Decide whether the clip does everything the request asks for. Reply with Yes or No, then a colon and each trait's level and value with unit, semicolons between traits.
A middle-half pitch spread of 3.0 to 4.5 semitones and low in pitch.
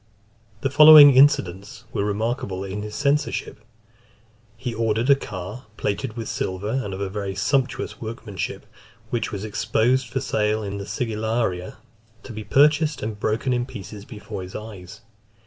Yes: average, 4.1 semitones; low, 110 Hz